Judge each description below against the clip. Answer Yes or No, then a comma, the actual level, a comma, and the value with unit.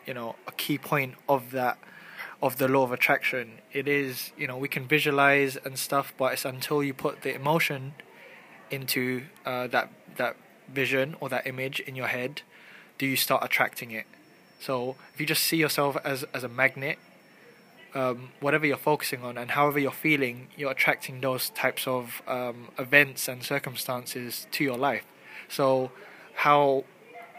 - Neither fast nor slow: Yes, average, 170 wpm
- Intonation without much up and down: Yes, narrow, 1.9 semitones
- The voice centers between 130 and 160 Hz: Yes, low, 135 Hz